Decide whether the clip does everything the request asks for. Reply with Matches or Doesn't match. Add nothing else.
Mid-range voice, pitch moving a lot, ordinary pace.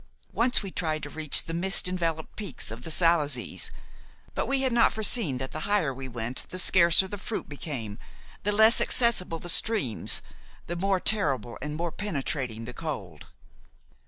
Matches